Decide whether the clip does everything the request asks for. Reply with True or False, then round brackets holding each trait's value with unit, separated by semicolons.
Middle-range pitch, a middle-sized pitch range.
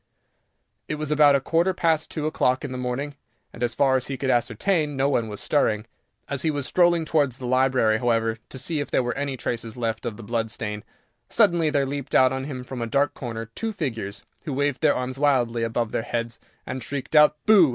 False (130 Hz; 3.8 semitones)